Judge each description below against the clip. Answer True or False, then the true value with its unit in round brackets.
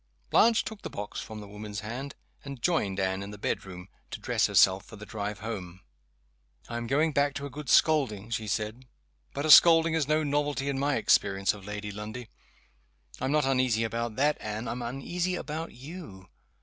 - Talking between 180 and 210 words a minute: True (190 wpm)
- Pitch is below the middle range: True (120 Hz)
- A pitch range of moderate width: False (5.8 semitones)